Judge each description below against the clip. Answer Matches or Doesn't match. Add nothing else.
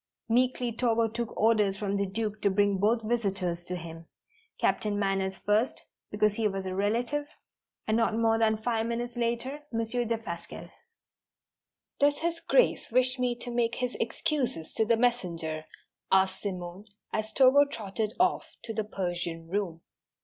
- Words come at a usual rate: Matches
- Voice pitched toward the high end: Matches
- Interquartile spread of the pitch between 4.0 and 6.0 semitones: Doesn't match